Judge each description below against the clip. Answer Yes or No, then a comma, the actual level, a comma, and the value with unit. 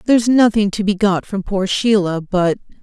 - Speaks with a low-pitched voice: No, high, 200 Hz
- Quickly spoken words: No, average, 190 wpm